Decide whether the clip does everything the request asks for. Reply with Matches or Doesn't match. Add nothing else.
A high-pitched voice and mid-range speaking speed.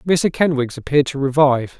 Doesn't match